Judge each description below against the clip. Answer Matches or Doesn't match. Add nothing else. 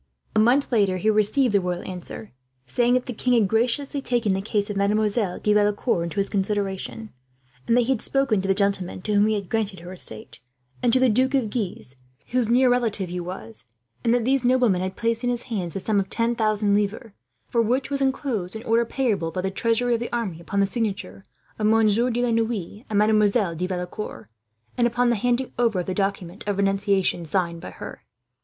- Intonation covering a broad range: Doesn't match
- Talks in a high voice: Matches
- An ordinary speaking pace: Doesn't match